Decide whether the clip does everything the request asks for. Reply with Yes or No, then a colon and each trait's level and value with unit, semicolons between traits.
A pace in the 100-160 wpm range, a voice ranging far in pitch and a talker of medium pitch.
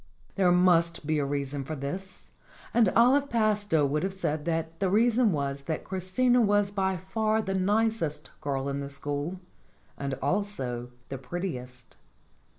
Yes: average, 155 wpm; wide, 6.3 semitones; medium, 175 Hz